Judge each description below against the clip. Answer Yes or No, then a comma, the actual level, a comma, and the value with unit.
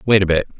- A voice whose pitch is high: No, very low, 95 Hz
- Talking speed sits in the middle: No, fast, 300 wpm